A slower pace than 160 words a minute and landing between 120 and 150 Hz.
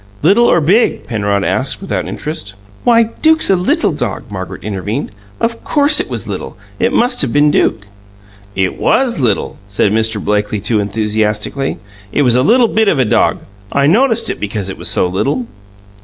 No: average, 185 wpm; low, 135 Hz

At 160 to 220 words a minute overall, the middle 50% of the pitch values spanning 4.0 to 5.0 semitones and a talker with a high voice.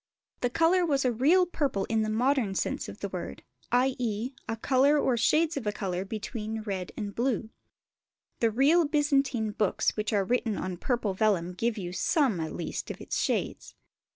Yes: average, 180 wpm; average, 4.7 semitones; high, 230 Hz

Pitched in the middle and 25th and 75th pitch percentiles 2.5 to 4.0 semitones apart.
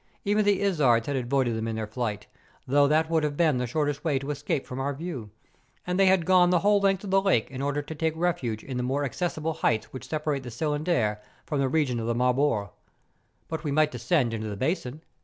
No: medium, 145 Hz; average, 4.7 semitones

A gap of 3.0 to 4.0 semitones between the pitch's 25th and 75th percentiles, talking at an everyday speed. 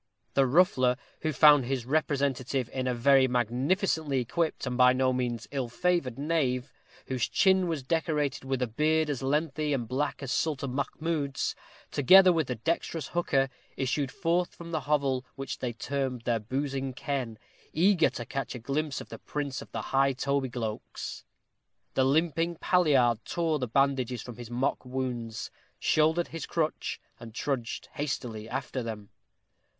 Yes: average, 3.6 semitones; average, 160 wpm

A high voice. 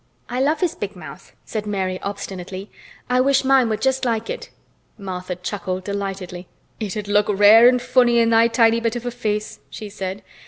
Yes: high, 215 Hz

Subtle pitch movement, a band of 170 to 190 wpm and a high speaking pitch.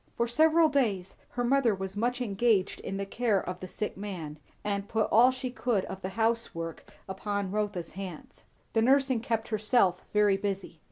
No: average, 3.9 semitones; average, 175 wpm; high, 210 Hz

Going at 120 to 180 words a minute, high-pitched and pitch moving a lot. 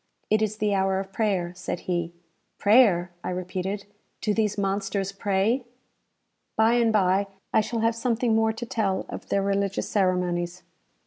No: average, 155 wpm; high, 200 Hz; average, 2.8 semitones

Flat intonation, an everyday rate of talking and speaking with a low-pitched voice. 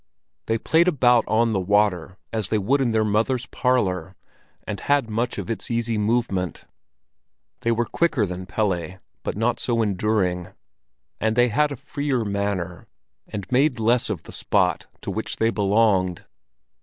No: average, 3.7 semitones; average, 160 wpm; low, 110 Hz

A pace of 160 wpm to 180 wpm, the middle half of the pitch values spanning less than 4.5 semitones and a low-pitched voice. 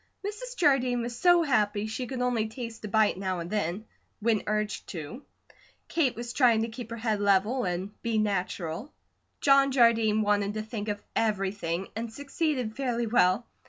No: average, 170 wpm; average, 3.3 semitones; high, 220 Hz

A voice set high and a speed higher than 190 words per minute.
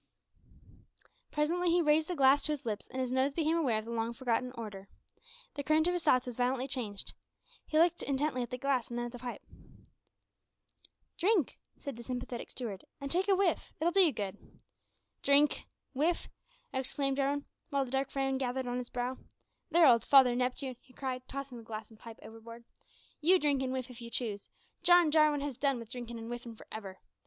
Yes: very high, 260 Hz; average, 200 wpm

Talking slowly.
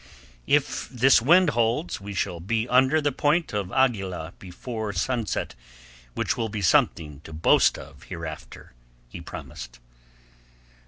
Yes: slow, 130 wpm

